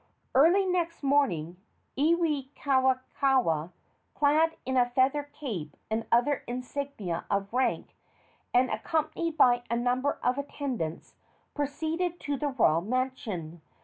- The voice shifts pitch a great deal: No, average, 3.6 semitones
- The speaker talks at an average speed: No, slow, 115 wpm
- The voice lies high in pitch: Yes, very high, 260 Hz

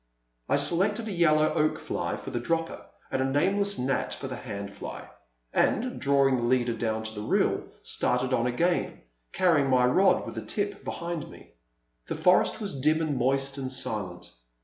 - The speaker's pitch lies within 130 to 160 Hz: Yes, low, 135 Hz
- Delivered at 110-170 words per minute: No, average, 180 wpm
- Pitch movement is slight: No, wide, 5.6 semitones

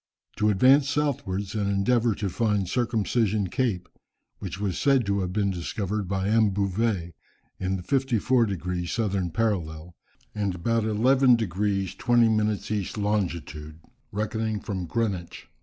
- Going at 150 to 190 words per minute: No, average, 140 wpm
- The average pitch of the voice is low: Yes, low, 105 Hz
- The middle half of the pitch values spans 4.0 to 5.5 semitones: No, average, 3.3 semitones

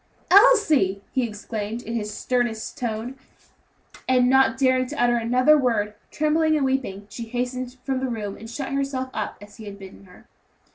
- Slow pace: No, average, 175 wpm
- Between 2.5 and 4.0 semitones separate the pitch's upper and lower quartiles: Yes, average, 3.5 semitones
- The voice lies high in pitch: Yes, high, 245 Hz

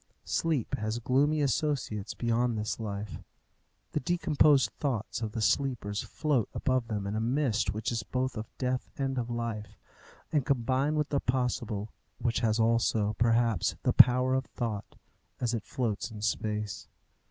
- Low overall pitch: Yes, low, 120 Hz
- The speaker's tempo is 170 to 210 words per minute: No, average, 155 wpm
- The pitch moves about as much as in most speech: Yes, average, 3.3 semitones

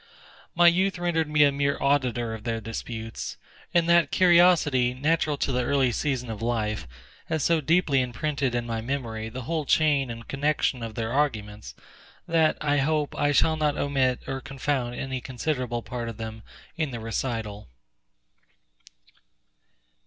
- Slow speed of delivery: No, average, 155 wpm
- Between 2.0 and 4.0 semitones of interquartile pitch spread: No, average, 4.4 semitones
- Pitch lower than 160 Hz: Yes, low, 135 Hz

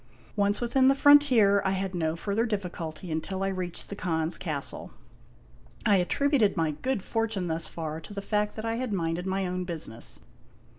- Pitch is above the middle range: Yes, high, 195 Hz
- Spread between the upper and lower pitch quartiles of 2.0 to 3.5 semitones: No, average, 4.5 semitones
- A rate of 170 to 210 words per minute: Yes, average, 180 wpm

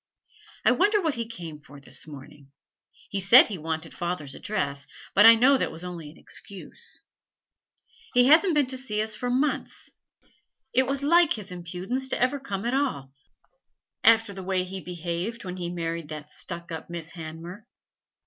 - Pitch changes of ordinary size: No, wide, 7.1 semitones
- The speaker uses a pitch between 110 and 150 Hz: No, high, 190 Hz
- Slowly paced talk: No, average, 175 wpm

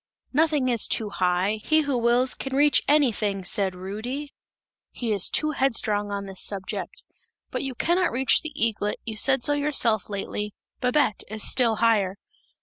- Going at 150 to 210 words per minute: Yes, average, 160 wpm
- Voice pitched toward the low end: No, high, 230 Hz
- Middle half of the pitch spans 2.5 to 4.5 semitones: No, average, 5.1 semitones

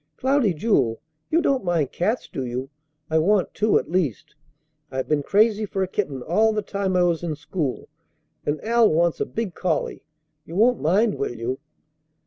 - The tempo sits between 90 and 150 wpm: No, average, 180 wpm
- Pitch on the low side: No, medium, 180 Hz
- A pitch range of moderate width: No, wide, 6.2 semitones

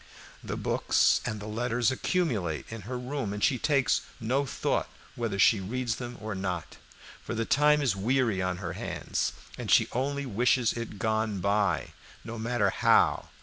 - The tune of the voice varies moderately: Yes, average, 3.8 semitones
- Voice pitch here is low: Yes, low, 115 Hz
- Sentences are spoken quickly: No, average, 165 wpm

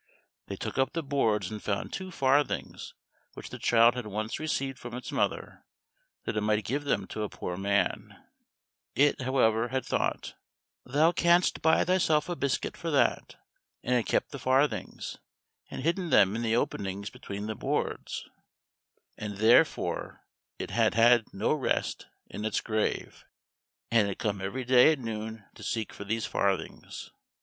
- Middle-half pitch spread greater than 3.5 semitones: Yes, average, 4.5 semitones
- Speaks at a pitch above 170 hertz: No, low, 120 Hz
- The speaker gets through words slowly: No, average, 165 wpm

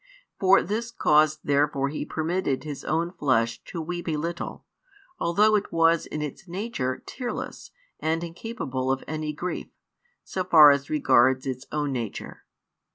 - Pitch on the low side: No, medium, 155 Hz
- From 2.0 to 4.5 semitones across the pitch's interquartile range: Yes, average, 4.0 semitones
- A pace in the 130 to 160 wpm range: Yes, average, 150 wpm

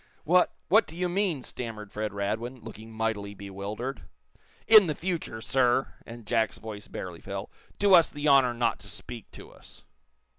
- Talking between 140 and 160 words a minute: No, average, 170 wpm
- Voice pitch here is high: No, low, 120 Hz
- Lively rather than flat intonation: Yes, wide, 5.9 semitones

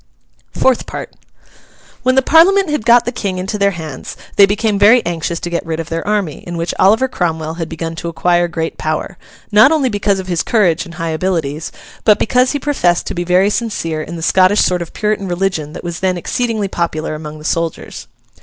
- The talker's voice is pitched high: No, medium, 180 Hz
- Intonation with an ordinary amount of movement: Yes, average, 4.4 semitones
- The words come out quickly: Yes, fast, 210 wpm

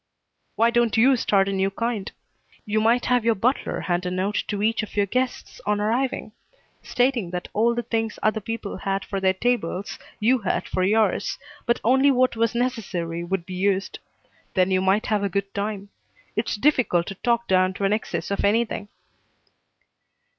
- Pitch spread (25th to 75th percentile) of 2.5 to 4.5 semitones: Yes, average, 3.4 semitones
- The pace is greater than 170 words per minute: Yes, average, 180 wpm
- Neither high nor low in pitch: No, high, 210 Hz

